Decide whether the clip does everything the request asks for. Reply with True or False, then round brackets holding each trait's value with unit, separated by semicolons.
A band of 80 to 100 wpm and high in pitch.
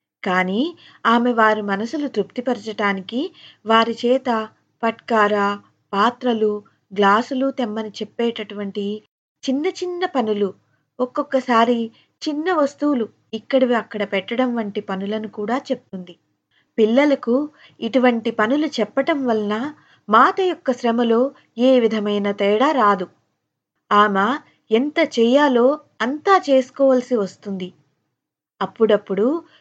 True (90 wpm; 230 Hz)